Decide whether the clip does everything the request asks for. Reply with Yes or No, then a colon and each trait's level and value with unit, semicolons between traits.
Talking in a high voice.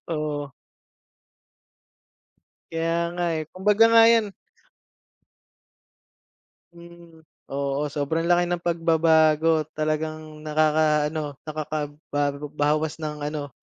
No: medium, 155 Hz